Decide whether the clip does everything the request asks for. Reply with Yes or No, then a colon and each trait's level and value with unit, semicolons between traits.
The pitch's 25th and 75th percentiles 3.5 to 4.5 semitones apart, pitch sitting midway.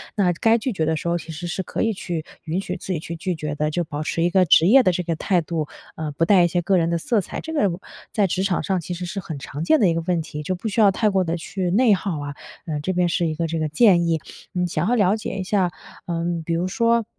No: average, 2.9 semitones; medium, 175 Hz